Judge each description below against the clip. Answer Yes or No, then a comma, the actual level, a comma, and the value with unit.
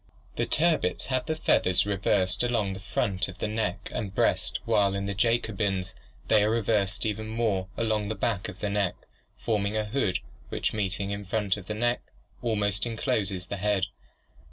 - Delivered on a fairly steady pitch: Yes, narrow, 2.3 semitones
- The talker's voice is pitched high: No, low, 105 Hz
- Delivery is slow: No, average, 180 wpm